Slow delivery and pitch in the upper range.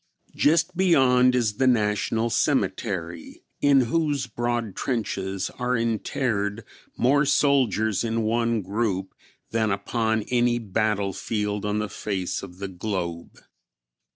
No: slow, 115 wpm; low, 110 Hz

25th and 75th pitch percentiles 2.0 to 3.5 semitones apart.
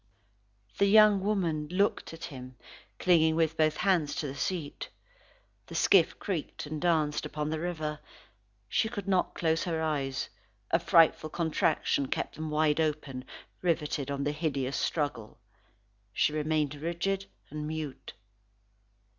Yes: narrow, 2.5 semitones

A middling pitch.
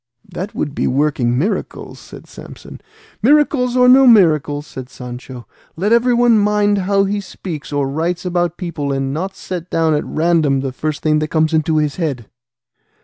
Yes: medium, 165 Hz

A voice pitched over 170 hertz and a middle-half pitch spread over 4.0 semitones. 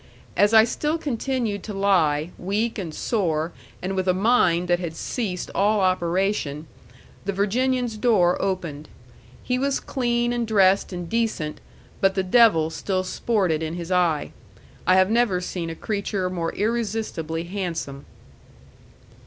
Yes: high, 190 Hz; average, 4.5 semitones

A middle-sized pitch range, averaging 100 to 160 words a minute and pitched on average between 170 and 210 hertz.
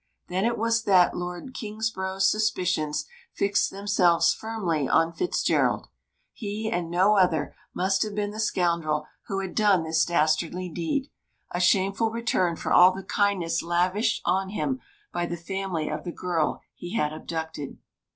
Yes: average, 3.5 semitones; average, 150 wpm; medium, 185 Hz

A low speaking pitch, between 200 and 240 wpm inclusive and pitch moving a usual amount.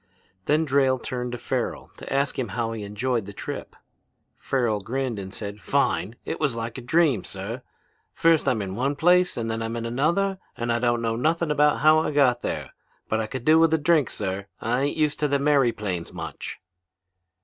Yes: low, 125 Hz; fast, 205 wpm; average, 4.7 semitones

